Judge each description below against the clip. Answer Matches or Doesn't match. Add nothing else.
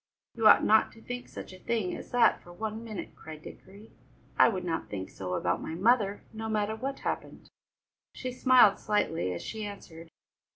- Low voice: Doesn't match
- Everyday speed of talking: Matches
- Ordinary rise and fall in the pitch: Matches